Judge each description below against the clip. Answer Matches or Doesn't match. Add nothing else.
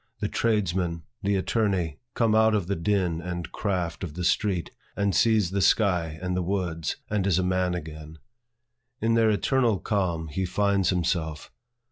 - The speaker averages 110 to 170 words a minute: Matches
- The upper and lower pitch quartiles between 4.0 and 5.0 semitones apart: Doesn't match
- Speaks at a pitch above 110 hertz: Doesn't match